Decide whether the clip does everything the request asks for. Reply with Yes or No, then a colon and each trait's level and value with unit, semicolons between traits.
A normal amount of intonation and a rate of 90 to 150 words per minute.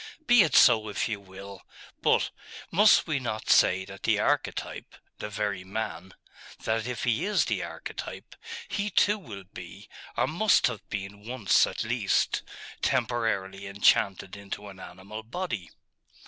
Yes: average, 4.0 semitones; average, 145 wpm